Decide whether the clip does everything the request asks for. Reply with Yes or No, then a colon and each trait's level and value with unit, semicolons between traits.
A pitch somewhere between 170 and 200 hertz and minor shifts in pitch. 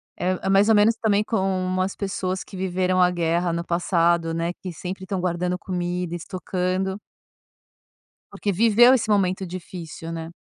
Yes: medium, 185 Hz; narrow, 1.8 semitones